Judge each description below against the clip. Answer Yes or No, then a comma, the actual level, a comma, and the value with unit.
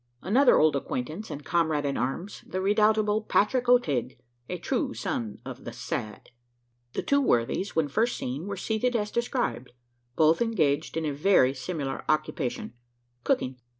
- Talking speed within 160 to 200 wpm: No, average, 150 wpm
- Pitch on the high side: No, medium, 165 Hz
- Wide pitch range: Yes, wide, 7.6 semitones